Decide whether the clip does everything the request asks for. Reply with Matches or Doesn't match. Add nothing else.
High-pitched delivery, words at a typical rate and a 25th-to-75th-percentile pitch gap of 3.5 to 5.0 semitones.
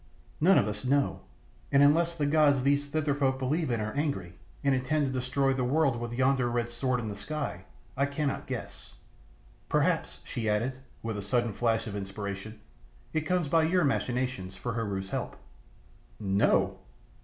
Doesn't match